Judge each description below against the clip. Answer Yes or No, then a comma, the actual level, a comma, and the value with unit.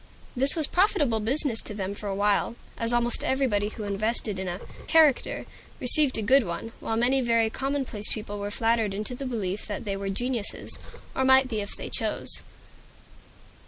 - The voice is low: No, high, 225 Hz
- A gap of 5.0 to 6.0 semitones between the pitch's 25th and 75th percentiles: No, average, 4.2 semitones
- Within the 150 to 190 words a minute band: Yes, average, 180 wpm